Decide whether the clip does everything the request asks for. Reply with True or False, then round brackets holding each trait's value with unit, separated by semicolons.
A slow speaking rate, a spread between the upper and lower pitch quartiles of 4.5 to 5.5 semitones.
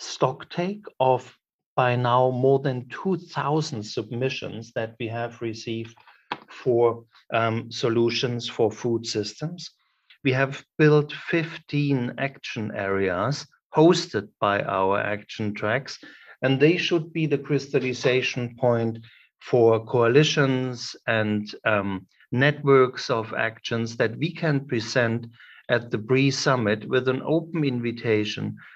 False (115 wpm; 3.6 semitones)